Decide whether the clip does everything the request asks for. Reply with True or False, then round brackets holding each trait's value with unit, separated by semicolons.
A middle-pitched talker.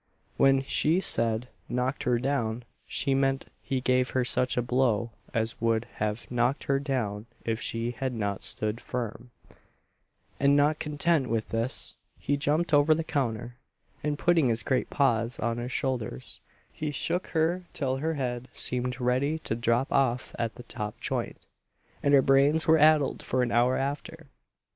False (130 Hz)